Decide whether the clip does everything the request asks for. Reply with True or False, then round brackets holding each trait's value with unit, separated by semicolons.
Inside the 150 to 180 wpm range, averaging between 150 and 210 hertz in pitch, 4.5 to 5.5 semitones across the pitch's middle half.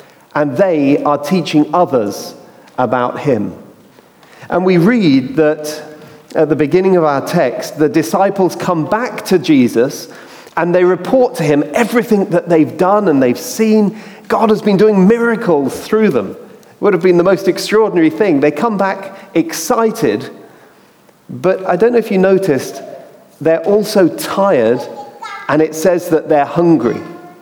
True (155 wpm; 185 Hz; 5.2 semitones)